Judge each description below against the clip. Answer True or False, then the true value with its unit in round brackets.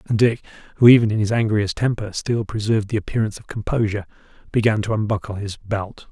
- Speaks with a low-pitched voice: True (105 Hz)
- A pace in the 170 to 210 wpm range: True (185 wpm)